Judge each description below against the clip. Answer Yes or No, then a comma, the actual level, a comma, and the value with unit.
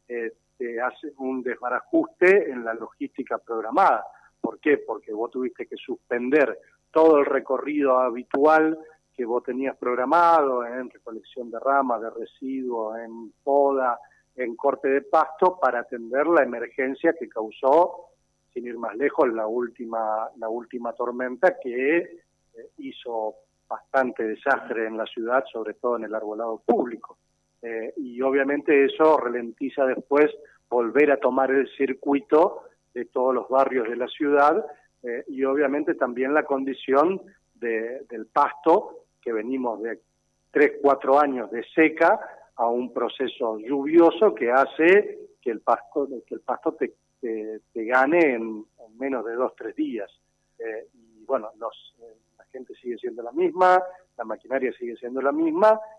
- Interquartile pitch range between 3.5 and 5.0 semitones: No, wide, 5.5 semitones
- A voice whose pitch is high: No, low, 135 Hz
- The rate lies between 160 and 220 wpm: No, average, 150 wpm